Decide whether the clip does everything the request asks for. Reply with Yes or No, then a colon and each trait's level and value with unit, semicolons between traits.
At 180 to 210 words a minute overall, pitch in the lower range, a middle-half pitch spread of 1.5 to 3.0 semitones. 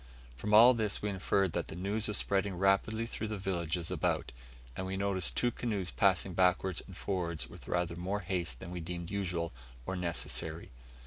Yes: average, 190 wpm; very low, 95 Hz; narrow, 2.6 semitones